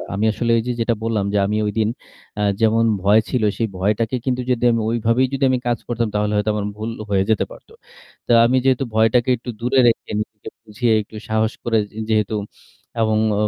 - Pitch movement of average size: No, narrow, 2.0 semitones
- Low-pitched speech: Yes, low, 110 Hz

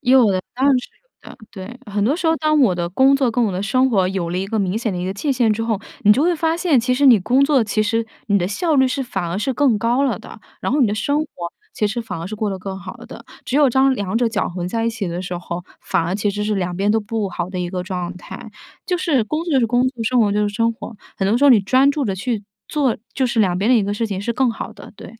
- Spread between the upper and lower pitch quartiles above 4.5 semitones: Yes, average, 5.0 semitones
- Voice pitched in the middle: No, high, 225 Hz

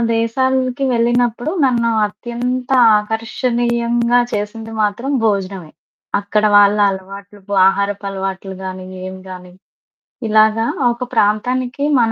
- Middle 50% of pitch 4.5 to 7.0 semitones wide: No, average, 3.1 semitones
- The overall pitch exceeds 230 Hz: No, high, 220 Hz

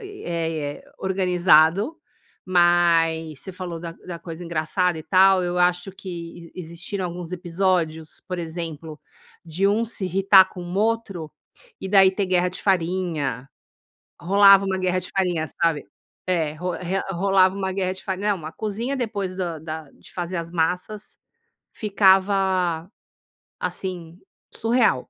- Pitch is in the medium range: Yes, medium, 180 Hz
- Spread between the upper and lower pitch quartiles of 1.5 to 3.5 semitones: Yes, narrow, 2.5 semitones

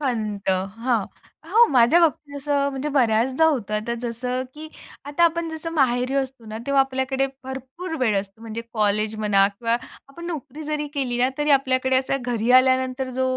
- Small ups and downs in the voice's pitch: No, average, 3.6 semitones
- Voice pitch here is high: Yes, very high, 260 Hz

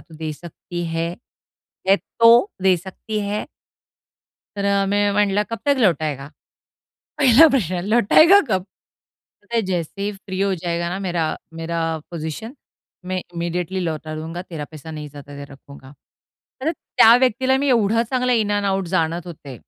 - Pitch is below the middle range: No, medium, 185 Hz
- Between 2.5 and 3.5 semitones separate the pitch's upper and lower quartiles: No, average, 4.7 semitones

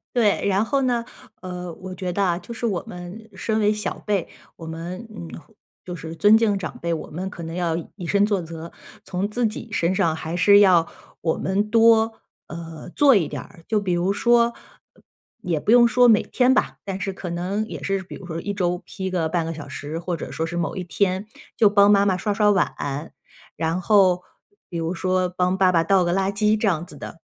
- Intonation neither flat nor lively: Yes, average, 3.4 semitones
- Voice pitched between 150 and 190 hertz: Yes, medium, 185 Hz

